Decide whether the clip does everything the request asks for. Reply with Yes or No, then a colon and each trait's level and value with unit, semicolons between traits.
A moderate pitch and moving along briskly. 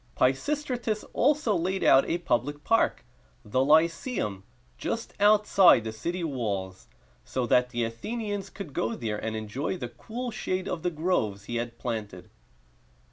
No: medium, 150 Hz; average, 150 wpm